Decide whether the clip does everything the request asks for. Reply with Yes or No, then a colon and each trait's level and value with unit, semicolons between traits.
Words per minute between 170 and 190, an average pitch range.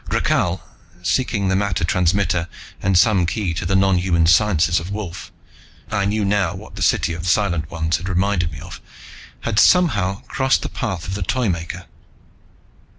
No: average, 160 wpm; average, 3.1 semitones